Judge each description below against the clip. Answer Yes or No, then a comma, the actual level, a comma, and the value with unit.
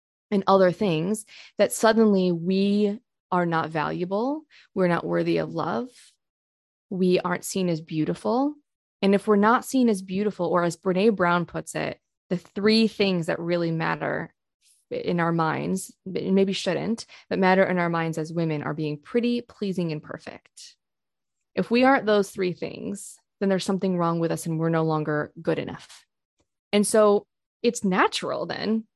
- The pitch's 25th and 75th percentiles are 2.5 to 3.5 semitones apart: No, average, 4.2 semitones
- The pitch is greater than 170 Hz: Yes, high, 190 Hz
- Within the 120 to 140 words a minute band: No, average, 165 wpm